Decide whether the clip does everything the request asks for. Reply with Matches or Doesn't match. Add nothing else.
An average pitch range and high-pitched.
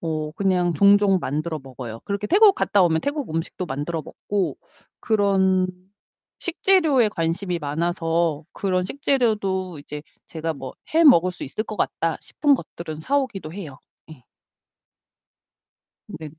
Doesn't match